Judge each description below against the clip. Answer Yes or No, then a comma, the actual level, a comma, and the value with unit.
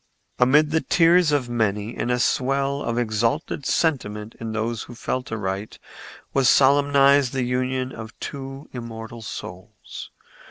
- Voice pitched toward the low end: Yes, low, 125 Hz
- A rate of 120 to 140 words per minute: Yes, slow, 135 wpm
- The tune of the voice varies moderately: Yes, average, 3.7 semitones